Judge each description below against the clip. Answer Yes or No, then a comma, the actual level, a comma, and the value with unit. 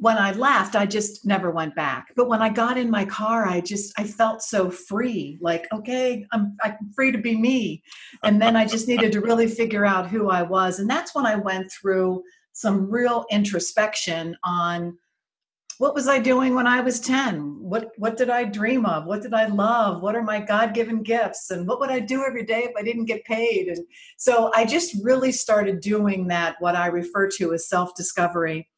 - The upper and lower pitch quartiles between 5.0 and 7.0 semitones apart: No, average, 3.7 semitones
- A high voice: Yes, high, 215 Hz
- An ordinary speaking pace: No, fast, 210 wpm